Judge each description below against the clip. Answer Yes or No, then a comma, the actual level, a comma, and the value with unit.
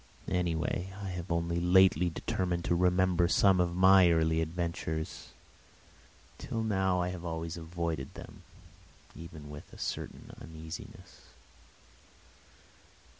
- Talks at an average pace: No, slow, 115 wpm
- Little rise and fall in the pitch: Yes, narrow, 1.9 semitones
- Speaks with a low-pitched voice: Yes, very low, 85 Hz